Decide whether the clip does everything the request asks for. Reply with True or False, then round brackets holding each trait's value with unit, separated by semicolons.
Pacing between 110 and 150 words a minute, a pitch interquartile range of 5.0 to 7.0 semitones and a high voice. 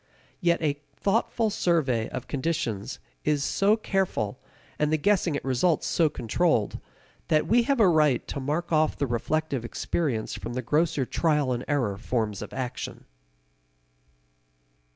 False (145 wpm; 5.5 semitones; 150 Hz)